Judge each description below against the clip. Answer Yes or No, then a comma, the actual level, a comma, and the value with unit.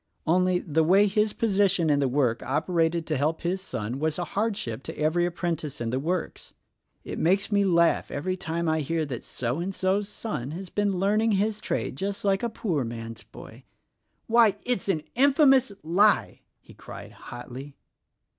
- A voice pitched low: No, medium, 175 Hz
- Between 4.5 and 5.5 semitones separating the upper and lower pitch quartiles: Yes, average, 5.2 semitones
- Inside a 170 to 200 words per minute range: Yes, average, 175 wpm